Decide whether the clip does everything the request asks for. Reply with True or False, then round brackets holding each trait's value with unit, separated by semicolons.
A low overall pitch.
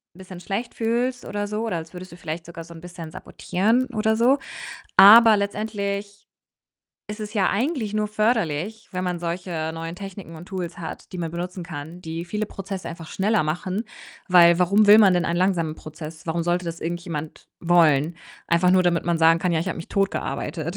False (180 Hz)